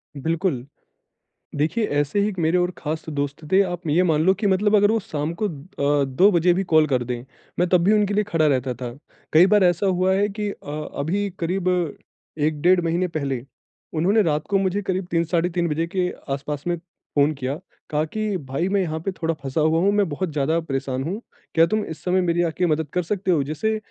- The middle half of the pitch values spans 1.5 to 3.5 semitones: No, average, 4.2 semitones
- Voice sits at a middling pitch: Yes, medium, 170 Hz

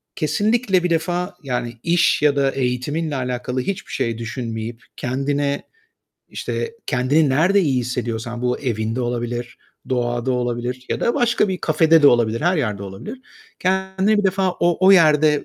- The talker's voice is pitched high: No, low, 135 Hz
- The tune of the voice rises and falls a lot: Yes, wide, 6.4 semitones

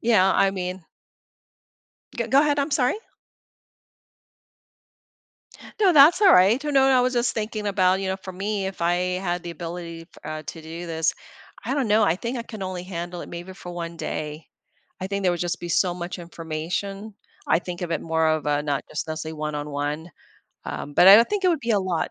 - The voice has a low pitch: No, medium, 180 Hz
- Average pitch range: Yes, average, 4.4 semitones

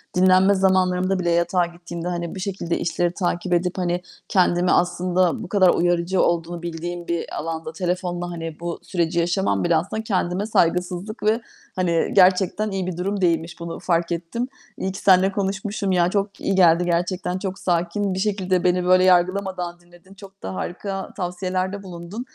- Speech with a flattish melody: Yes, narrow, 1.7 semitones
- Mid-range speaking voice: Yes, medium, 180 Hz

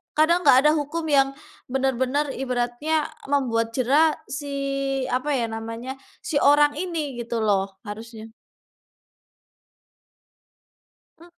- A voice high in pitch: Yes, very high, 270 Hz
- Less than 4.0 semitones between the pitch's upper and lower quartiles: Yes, average, 3.6 semitones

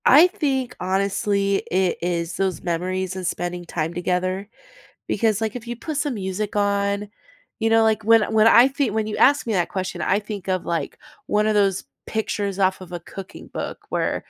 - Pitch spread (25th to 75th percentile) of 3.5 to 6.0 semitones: No, average, 3.1 semitones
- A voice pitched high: Yes, high, 200 Hz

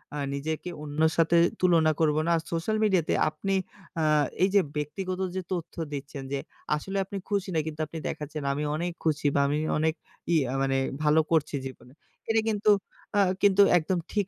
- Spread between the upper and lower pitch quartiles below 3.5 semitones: No, average, 3.9 semitones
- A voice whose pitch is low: No, medium, 160 Hz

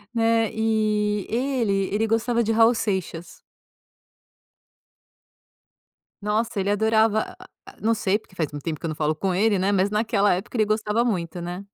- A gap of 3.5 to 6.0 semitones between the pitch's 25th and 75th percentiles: No, average, 2.9 semitones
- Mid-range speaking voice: No, high, 210 Hz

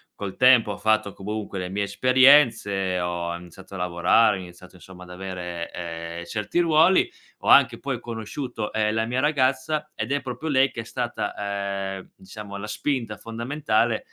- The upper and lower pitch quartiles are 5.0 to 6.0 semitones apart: Yes, wide, 5.6 semitones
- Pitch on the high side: No, low, 105 Hz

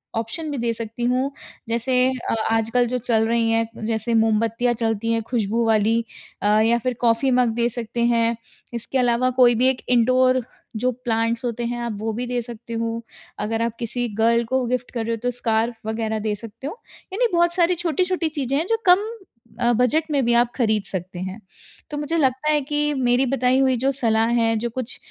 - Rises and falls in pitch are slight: Yes, narrow, 2.2 semitones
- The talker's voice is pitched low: No, high, 235 Hz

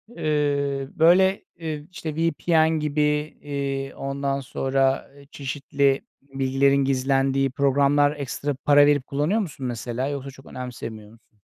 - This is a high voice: No, medium, 140 Hz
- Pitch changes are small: Yes, narrow, 1.6 semitones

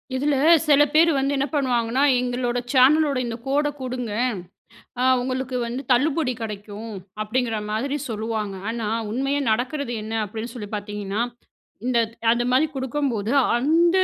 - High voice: Yes, very high, 250 Hz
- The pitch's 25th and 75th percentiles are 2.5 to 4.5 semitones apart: Yes, average, 3.6 semitones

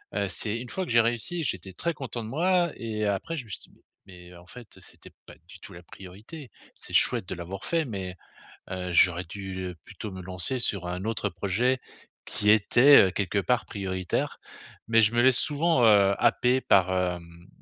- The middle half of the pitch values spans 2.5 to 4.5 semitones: No, average, 5.0 semitones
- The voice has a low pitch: Yes, low, 105 Hz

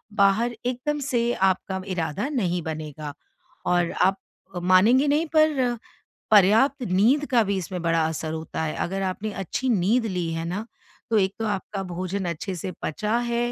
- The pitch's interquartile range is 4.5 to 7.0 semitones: Yes, average, 5.2 semitones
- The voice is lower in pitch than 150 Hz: No, high, 195 Hz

